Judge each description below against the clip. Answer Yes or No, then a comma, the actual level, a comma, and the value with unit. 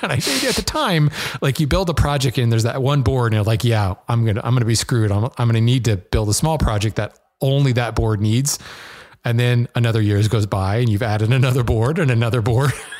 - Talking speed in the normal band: No, fast, 255 wpm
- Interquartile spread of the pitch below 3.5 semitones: Yes, average, 3.1 semitones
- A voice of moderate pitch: No, low, 120 Hz